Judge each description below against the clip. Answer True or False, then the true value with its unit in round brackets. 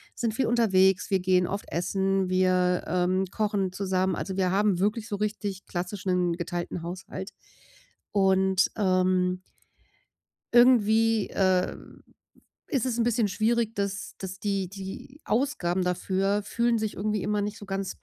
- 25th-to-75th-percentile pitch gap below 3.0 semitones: True (2.4 semitones)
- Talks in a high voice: True (195 Hz)